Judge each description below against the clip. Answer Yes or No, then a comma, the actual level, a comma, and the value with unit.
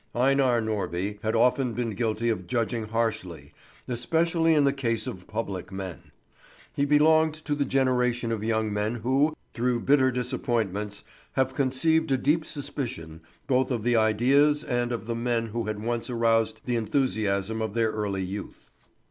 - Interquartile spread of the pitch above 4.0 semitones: No, average, 3.5 semitones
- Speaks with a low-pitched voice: Yes, low, 120 Hz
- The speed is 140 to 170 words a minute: Yes, average, 160 wpm